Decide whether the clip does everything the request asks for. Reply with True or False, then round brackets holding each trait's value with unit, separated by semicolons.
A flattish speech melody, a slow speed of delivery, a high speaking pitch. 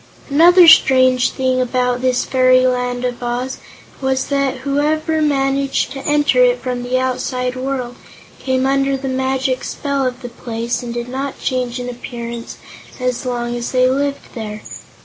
False (1.7 semitones; 160 wpm; 255 Hz)